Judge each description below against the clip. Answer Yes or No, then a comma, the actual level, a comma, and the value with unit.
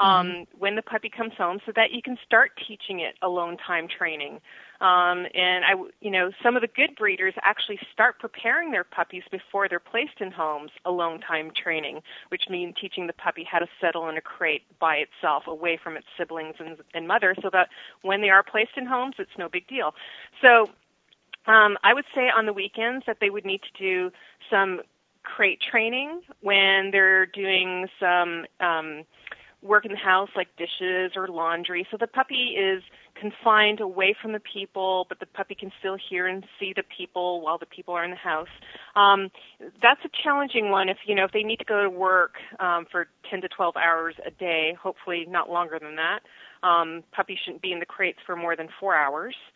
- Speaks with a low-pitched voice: No, high, 190 Hz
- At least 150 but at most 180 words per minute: No, fast, 205 wpm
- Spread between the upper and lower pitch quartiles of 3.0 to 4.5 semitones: Yes, average, 3.6 semitones